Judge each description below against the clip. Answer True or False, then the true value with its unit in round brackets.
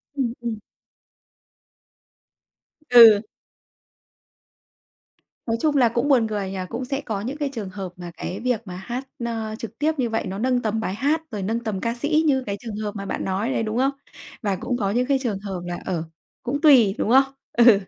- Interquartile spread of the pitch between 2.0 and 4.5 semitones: True (4.1 semitones)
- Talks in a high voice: True (230 Hz)